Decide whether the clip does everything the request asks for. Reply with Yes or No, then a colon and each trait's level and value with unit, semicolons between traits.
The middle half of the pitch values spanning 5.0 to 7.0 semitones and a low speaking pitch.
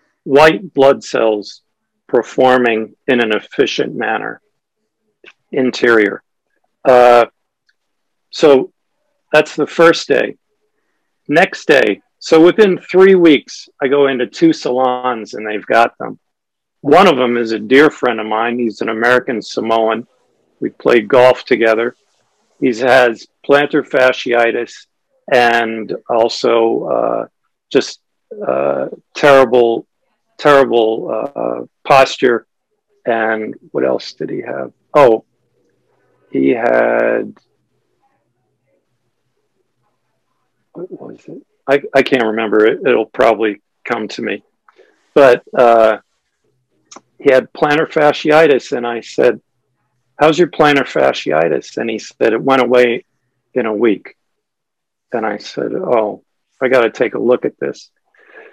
Yes: average, 5.3 semitones; low, 125 Hz